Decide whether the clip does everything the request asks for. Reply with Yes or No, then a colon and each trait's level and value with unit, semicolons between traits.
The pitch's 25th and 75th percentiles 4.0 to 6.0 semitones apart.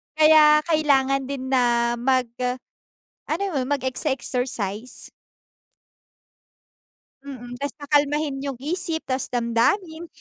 No: average, 3.4 semitones